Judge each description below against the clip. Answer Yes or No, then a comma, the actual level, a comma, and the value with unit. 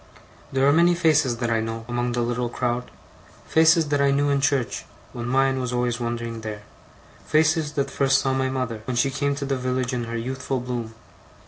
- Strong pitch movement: No, narrow, 2.6 semitones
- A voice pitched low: Yes, low, 130 Hz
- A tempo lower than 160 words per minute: No, fast, 205 wpm